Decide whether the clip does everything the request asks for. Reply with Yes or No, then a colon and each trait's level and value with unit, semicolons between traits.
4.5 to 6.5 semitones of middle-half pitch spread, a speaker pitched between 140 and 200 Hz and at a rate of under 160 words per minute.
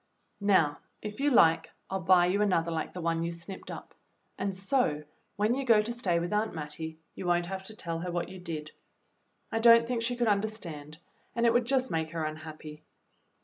No: average, 5.2 semitones; medium, 185 Hz; fast, 205 wpm